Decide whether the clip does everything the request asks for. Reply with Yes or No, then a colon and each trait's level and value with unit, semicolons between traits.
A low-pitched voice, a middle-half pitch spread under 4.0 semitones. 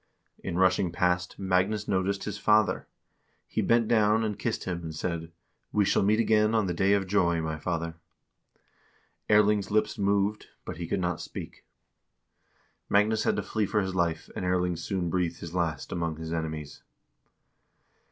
Yes: very low, 95 Hz; average, 3.5 semitones